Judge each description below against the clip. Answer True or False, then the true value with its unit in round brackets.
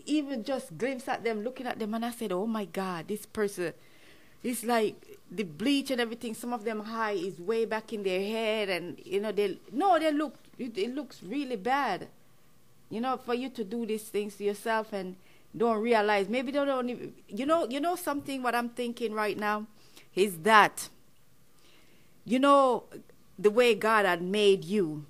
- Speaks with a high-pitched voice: True (225 Hz)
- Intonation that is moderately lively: True (3.4 semitones)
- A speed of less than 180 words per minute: False (195 wpm)